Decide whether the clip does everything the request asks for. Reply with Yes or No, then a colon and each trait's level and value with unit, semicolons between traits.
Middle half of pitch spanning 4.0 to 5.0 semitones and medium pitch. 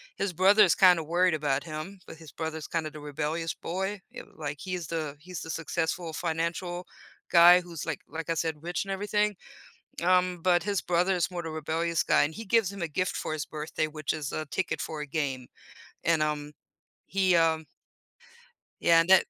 No: average, 2.7 semitones; medium, 165 Hz